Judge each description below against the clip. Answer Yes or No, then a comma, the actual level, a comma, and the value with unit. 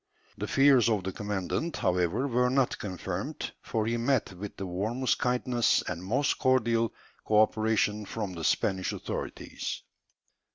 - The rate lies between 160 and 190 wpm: No, average, 140 wpm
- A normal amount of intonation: Yes, average, 4.6 semitones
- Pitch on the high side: No, low, 110 Hz